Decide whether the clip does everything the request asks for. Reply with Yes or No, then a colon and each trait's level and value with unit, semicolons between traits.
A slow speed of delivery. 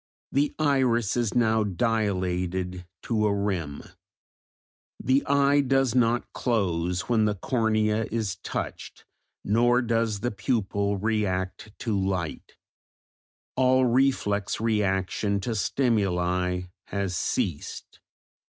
Yes: slow, 105 wpm